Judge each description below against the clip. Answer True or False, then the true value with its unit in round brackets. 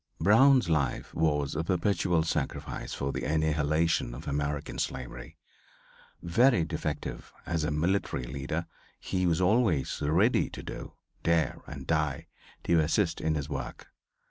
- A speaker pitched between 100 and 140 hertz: False (80 Hz)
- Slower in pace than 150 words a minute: True (135 wpm)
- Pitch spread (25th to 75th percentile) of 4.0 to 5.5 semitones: False (2.9 semitones)